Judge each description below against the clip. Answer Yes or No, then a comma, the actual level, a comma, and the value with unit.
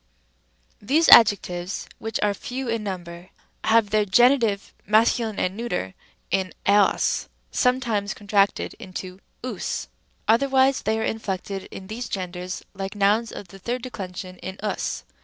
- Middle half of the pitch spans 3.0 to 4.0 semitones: Yes, average, 3.4 semitones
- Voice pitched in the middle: No, high, 205 Hz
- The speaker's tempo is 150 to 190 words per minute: No, average, 140 wpm